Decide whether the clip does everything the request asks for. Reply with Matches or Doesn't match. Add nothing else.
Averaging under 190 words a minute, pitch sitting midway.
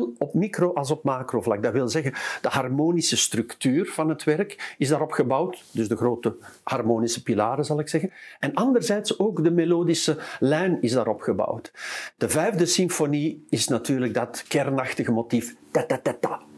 Matches